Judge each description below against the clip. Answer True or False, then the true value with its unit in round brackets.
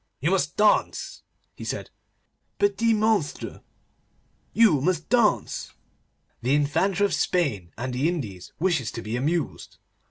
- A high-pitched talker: False (160 Hz)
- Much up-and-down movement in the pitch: True (7.5 semitones)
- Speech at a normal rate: False (125 wpm)